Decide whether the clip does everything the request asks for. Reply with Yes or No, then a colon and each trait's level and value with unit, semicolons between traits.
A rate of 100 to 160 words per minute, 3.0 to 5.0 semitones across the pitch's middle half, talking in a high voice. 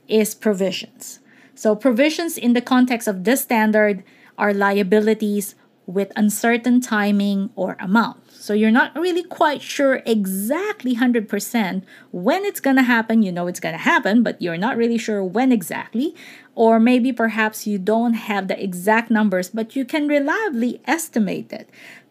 Yes: average, 150 wpm; average, 3.4 semitones; high, 225 Hz